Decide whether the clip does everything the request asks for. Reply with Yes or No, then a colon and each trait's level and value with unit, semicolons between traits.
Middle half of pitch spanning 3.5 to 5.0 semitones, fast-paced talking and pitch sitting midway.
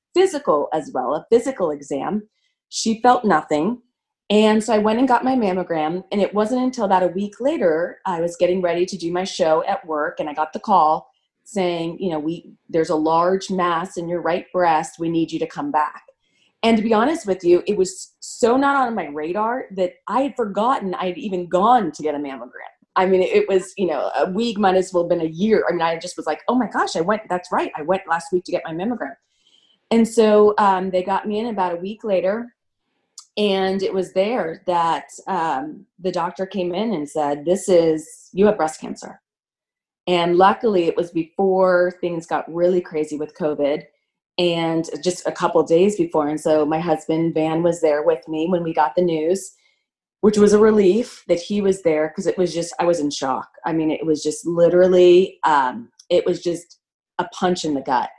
Yes: average, 4.1 semitones; fast, 215 wpm; medium, 180 Hz